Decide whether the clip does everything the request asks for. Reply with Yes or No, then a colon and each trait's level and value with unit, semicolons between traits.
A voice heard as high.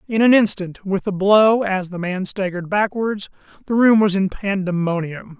Yes: high, 195 Hz